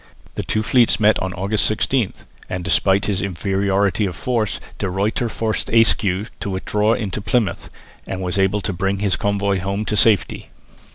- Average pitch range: No, narrow, 2.0 semitones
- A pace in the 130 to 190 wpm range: Yes, average, 170 wpm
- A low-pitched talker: Yes, low, 100 Hz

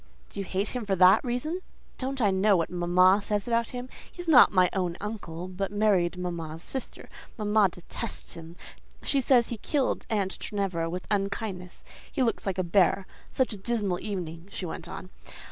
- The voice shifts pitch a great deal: No, average, 3.7 semitones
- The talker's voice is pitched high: Yes, high, 195 Hz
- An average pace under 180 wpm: No, average, 185 wpm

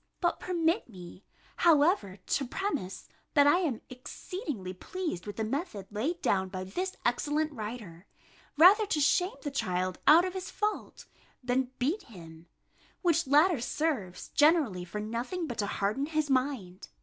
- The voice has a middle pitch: No, very high, 270 Hz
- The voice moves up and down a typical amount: No, wide, 8.6 semitones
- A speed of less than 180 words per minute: Yes, average, 150 wpm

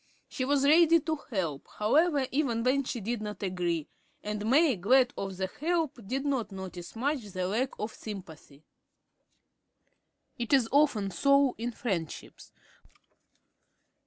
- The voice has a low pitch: No, high, 235 Hz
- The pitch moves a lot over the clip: Yes, wide, 6.2 semitones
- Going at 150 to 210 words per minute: No, slow, 135 wpm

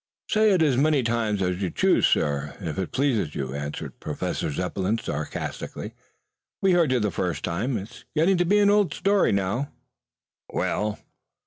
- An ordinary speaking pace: Yes, average, 165 wpm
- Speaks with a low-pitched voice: Yes, low, 110 Hz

